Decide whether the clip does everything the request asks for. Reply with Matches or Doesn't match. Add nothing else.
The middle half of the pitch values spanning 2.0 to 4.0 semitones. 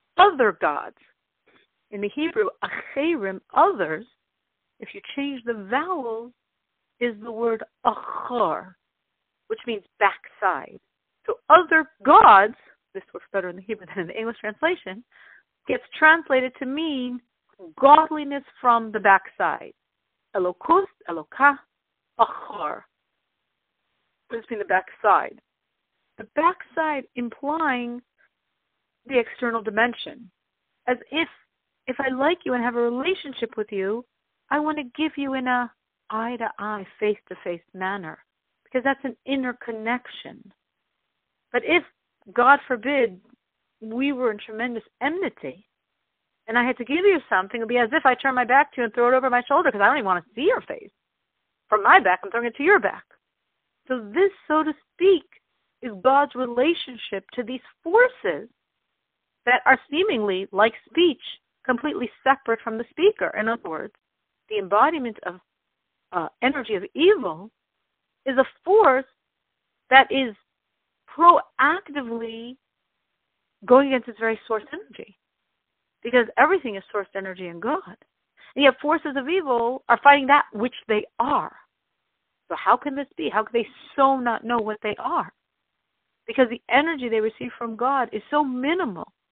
Doesn't match